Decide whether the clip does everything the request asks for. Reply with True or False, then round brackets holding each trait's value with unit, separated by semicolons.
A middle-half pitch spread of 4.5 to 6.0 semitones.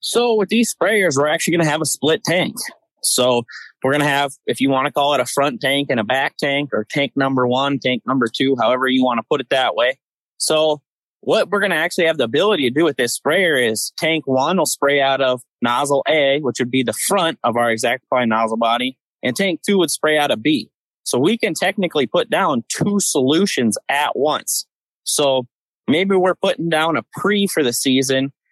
False (4.1 semitones)